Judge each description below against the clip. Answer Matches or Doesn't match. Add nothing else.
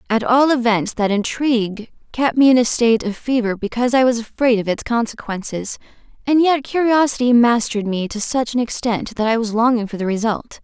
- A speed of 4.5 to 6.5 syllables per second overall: Matches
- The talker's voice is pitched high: Matches